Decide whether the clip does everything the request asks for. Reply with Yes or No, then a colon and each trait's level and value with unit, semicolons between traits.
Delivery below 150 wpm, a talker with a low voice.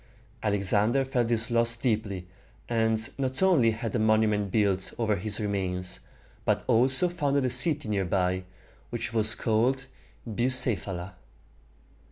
Yes: average, 140 wpm; low, 110 Hz